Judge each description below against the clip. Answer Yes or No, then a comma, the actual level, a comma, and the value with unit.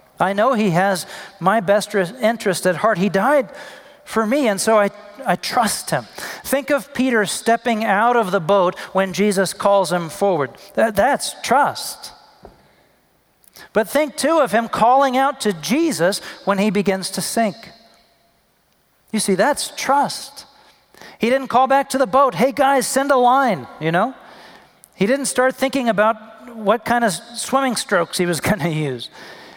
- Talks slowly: No, average, 165 wpm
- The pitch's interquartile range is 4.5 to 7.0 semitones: Yes, average, 5.2 semitones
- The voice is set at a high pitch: Yes, high, 225 Hz